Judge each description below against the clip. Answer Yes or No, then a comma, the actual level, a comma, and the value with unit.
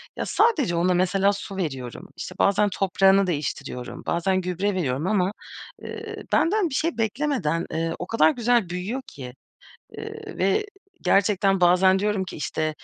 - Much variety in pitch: No, average, 3.4 semitones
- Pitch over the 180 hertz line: Yes, high, 190 Hz